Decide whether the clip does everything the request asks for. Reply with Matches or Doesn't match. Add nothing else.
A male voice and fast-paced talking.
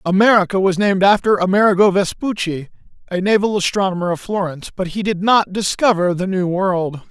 Doesn't match